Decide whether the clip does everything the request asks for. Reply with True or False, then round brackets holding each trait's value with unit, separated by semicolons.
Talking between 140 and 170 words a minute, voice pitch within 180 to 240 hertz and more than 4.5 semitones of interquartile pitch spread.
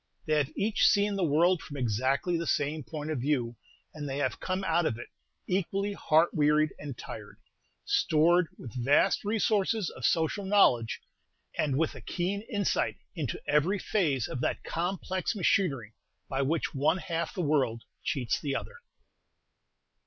False (160 wpm; 155 Hz; 5.1 semitones)